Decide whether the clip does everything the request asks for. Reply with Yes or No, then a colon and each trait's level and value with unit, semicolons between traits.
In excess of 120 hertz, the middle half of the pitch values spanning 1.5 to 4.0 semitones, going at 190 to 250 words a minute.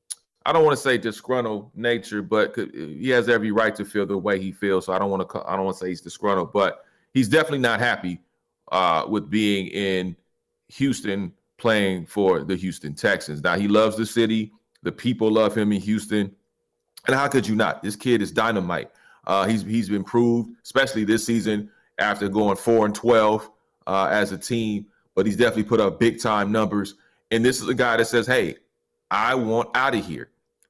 No: low, 110 Hz; average, 2.8 semitones; average, 200 wpm